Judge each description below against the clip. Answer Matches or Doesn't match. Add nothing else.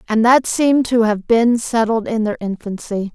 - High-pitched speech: Matches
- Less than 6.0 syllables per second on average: Matches